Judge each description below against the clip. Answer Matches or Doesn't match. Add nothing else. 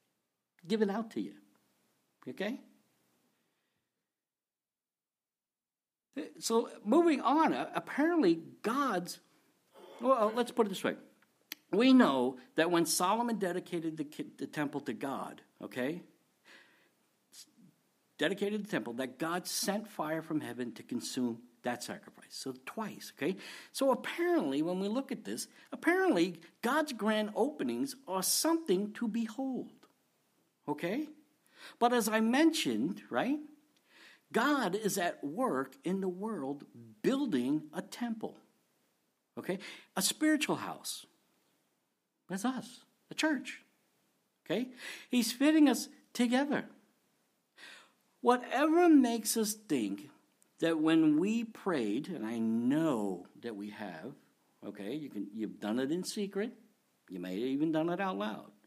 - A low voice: Doesn't match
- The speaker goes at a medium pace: Doesn't match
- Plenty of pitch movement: Matches